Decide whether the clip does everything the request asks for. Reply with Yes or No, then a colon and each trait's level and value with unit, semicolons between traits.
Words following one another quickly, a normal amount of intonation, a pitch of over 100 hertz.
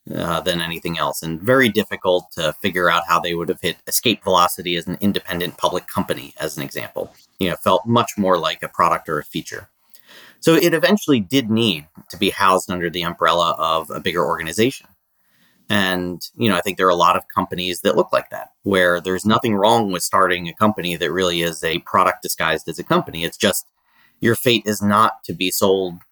No: fast, 210 wpm; average, 3.7 semitones; very low, 95 Hz